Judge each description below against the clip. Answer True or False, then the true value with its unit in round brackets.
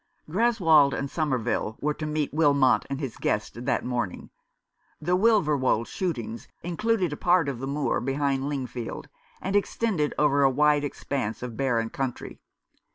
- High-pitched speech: False (140 Hz)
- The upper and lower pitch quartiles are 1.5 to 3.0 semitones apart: False (3.9 semitones)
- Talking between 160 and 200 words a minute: False (150 wpm)